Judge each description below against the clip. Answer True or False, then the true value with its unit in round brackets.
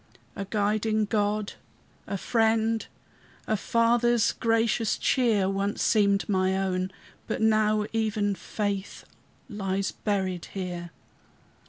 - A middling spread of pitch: False (2.2 semitones)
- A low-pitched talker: False (210 Hz)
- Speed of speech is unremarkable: False (105 wpm)